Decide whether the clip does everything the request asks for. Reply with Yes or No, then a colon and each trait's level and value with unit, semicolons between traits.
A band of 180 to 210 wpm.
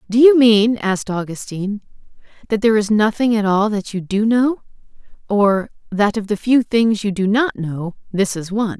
Yes: average, 190 wpm